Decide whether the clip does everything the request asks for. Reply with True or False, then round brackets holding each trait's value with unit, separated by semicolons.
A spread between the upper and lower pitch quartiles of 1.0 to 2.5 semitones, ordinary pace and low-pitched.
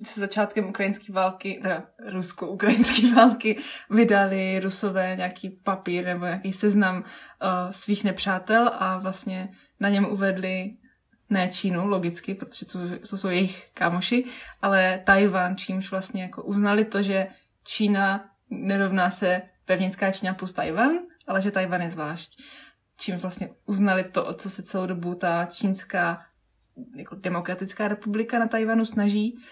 False (2.0 semitones; 140 wpm; 195 Hz)